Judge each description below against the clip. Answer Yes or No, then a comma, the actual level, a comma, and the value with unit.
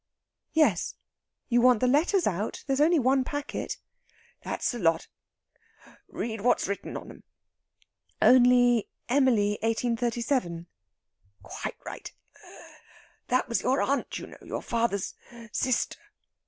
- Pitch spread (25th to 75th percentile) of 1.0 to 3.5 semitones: Yes, average, 3.0 semitones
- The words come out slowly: Yes, slow, 115 wpm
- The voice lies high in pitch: Yes, high, 245 Hz